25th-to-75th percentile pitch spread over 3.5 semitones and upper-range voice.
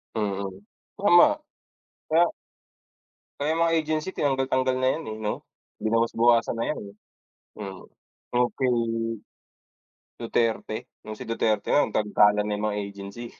No: average, 4.1 semitones; low, 115 Hz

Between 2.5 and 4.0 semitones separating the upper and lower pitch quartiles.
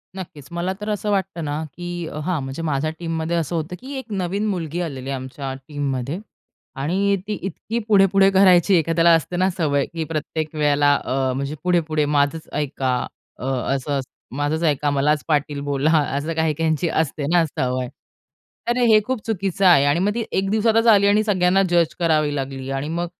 No: average, 4.4 semitones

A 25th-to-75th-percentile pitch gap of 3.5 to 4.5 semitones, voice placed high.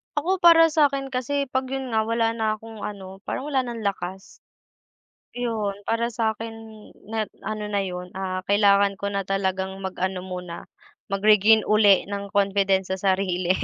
No: average, 3.0 semitones; high, 210 Hz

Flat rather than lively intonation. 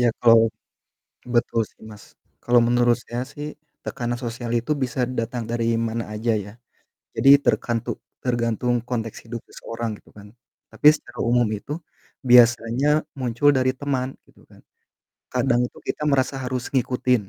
Yes: narrow, 1.5 semitones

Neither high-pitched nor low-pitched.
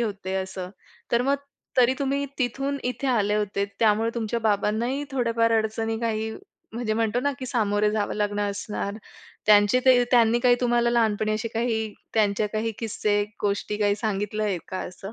No: high, 220 Hz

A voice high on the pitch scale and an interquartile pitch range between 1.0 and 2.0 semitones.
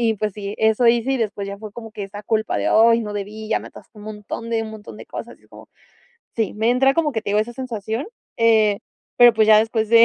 Yes: high, 220 Hz; narrow, 1.7 semitones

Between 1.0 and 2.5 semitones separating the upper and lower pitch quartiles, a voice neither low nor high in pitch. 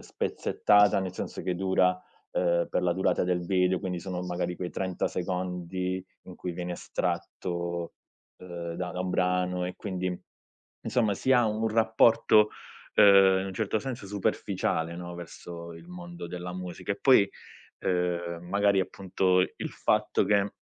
No: narrow, 1.9 semitones; very low, 90 Hz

